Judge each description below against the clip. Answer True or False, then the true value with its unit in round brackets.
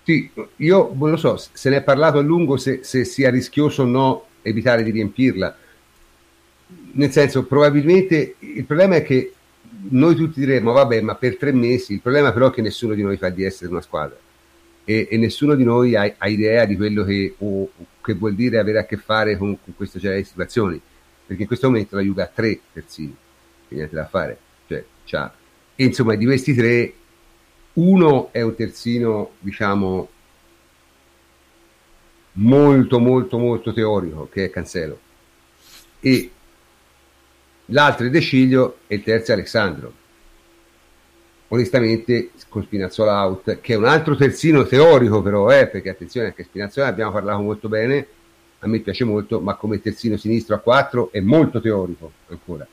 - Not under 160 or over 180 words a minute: True (165 wpm)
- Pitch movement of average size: False (7.0 semitones)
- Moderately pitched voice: False (110 Hz)